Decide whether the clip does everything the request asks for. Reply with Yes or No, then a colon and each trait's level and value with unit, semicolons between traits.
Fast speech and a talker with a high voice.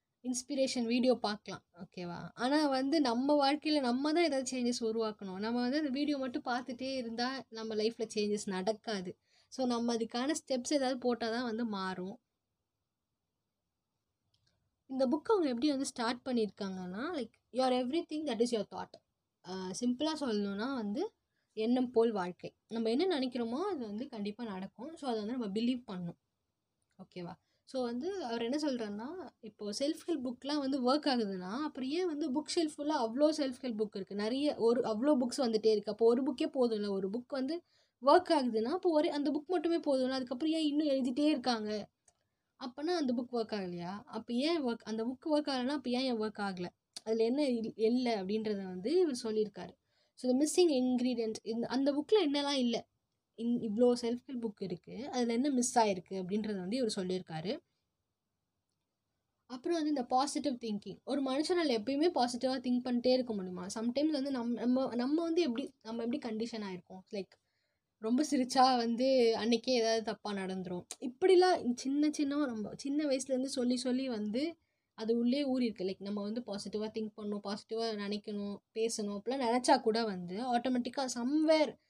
Yes: fast, 165 wpm; high, 245 Hz